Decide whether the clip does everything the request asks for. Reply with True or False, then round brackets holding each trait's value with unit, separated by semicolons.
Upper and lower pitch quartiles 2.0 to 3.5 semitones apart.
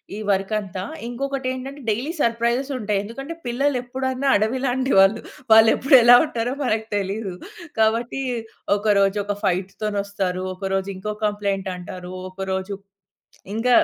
False (4.2 semitones)